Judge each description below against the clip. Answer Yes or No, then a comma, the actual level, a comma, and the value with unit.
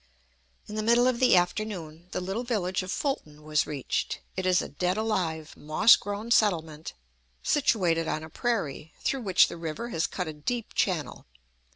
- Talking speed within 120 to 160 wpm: No, average, 175 wpm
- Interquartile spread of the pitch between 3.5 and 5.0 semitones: No, wide, 5.6 semitones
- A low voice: No, medium, 185 Hz